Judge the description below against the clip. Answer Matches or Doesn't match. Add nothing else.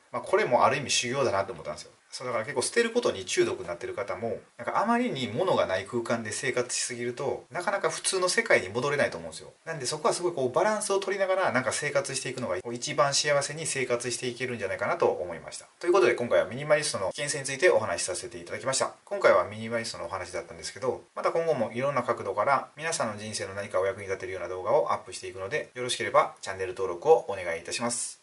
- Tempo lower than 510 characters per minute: Doesn't match